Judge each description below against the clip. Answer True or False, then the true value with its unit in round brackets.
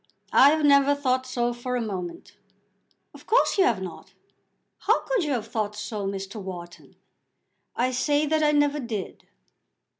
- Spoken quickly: False (160 wpm)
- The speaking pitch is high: True (250 Hz)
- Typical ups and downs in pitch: False (5.8 semitones)